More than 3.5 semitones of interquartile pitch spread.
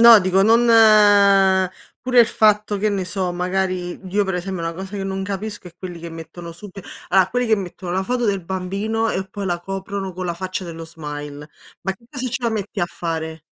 No: average, 2.9 semitones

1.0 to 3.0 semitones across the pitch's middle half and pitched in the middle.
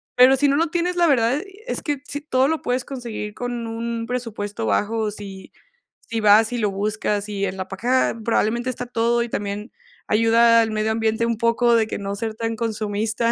No: narrow, 2.6 semitones; high, 230 Hz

